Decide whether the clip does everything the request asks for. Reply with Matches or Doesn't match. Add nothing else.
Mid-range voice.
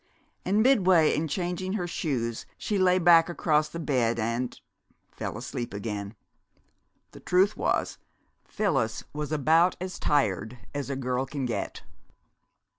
Matches